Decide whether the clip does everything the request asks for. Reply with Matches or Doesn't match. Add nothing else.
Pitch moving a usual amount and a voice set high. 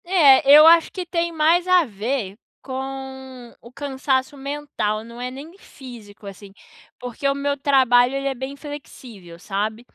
Matches